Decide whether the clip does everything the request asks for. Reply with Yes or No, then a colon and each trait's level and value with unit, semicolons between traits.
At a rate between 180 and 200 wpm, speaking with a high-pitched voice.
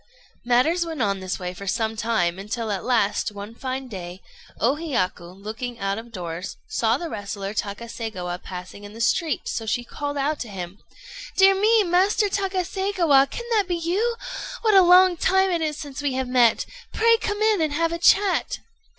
Yes: average, 190 wpm; very high, 255 Hz